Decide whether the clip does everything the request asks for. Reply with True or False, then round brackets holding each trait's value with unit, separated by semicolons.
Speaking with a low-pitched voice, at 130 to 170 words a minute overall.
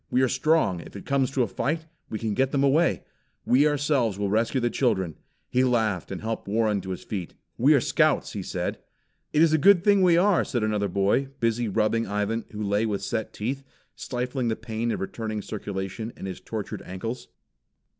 False (115 Hz; 205 wpm)